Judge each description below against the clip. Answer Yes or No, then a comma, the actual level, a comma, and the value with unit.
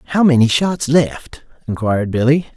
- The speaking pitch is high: No, low, 135 Hz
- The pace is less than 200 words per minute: Yes, average, 140 wpm